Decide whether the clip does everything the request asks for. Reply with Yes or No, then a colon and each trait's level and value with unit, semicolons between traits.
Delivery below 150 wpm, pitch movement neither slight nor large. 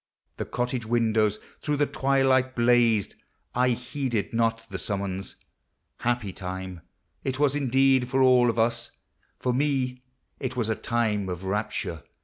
Yes: average, 140 wpm; average, 3.4 semitones